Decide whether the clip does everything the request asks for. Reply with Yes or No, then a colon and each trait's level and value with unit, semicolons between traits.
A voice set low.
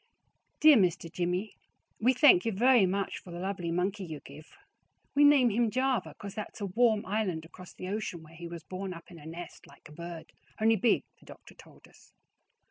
No: high, 190 Hz